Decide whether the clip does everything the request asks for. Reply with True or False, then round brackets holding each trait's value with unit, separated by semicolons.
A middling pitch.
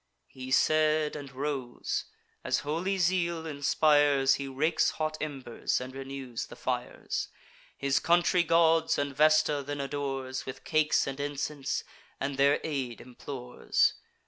True (145 Hz)